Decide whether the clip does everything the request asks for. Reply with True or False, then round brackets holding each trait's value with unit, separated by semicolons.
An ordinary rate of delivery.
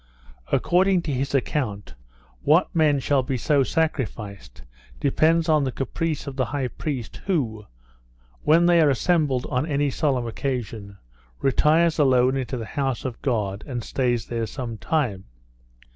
True (145 wpm)